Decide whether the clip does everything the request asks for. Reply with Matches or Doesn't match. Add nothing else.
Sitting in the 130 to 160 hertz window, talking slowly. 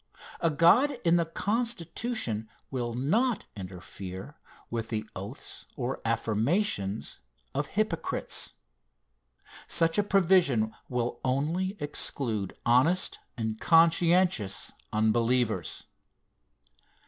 Matches